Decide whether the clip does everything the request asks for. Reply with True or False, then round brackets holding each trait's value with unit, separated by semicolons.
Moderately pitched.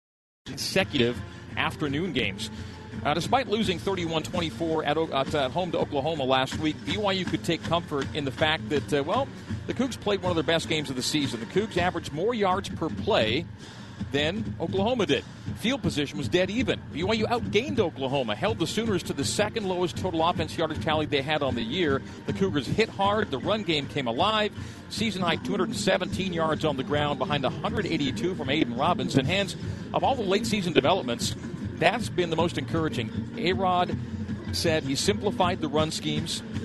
True (155 Hz)